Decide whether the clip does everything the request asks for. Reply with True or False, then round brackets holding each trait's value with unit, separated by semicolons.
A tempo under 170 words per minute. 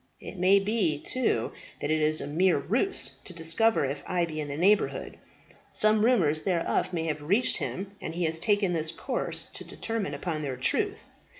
False (190 wpm)